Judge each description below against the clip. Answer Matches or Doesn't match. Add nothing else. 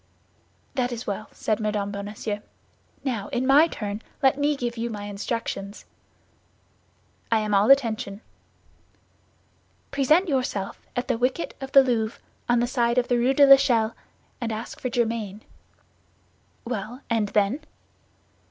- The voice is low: Doesn't match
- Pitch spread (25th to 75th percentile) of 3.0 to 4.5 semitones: Matches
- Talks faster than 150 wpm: Doesn't match